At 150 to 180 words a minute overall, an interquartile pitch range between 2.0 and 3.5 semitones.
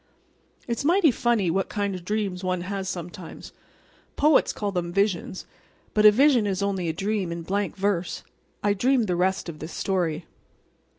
Yes: average, 170 wpm; average, 2.9 semitones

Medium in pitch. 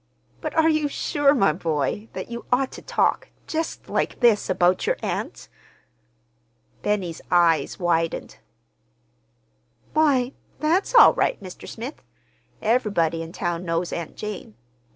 No: high, 205 Hz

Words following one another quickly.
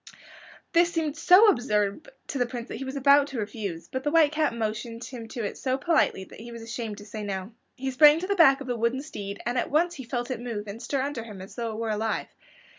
Yes: fast, 260 wpm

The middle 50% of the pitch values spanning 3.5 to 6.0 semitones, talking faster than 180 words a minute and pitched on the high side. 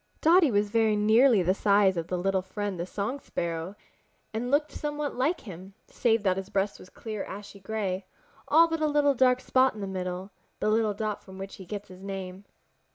Yes: average, 4.5 semitones; average, 200 wpm; high, 205 Hz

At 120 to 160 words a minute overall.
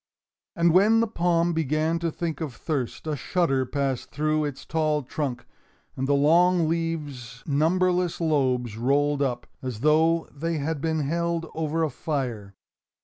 Yes: average, 150 wpm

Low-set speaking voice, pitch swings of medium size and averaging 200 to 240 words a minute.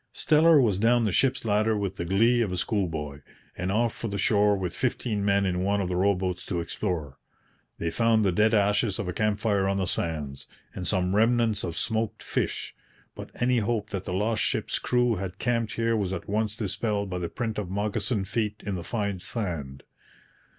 Yes: low, 100 Hz; average, 3.5 semitones; fast, 205 wpm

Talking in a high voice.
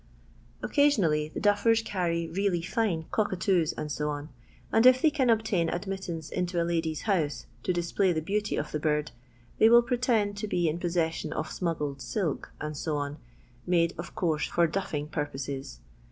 No: medium, 175 Hz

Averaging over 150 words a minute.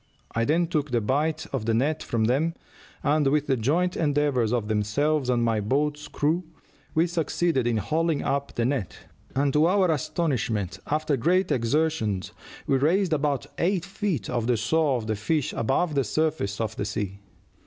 Yes: average, 175 wpm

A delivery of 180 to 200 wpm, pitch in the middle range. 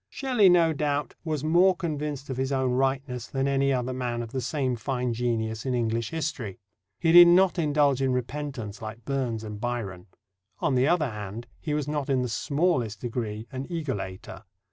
No: average, 185 wpm; low, 130 Hz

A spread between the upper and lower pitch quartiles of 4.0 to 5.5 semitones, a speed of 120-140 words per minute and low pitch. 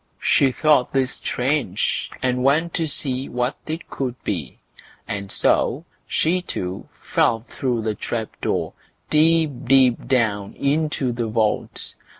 Yes: average, 4.5 semitones; slow, 135 wpm; low, 130 Hz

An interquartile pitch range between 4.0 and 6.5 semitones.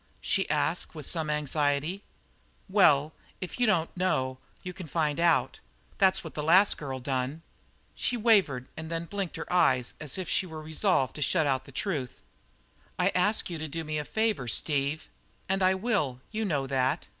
Yes: average, 4.9 semitones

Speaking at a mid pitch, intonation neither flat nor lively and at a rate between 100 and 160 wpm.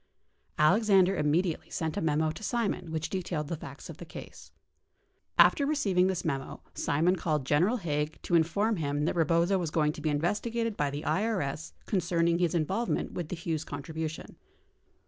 No: medium, 165 Hz; average, 3.7 semitones; average, 170 wpm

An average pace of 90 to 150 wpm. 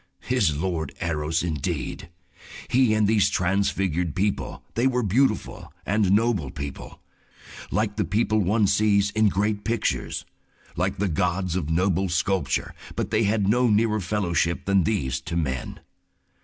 Yes: average, 140 wpm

